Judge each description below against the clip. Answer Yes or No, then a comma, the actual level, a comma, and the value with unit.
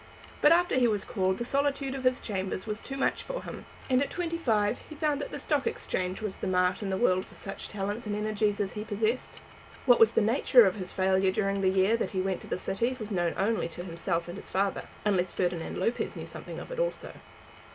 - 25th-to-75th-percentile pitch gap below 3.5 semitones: No, average, 5.1 semitones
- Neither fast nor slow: No, fast, 240 wpm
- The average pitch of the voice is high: Yes, high, 210 Hz